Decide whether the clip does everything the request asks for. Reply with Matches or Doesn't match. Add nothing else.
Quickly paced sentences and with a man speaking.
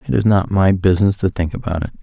Matches